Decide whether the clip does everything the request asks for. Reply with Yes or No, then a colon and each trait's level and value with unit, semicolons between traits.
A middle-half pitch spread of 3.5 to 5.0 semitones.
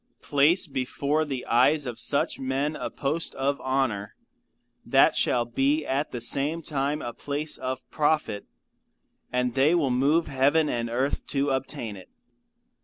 No: average, 2.8 semitones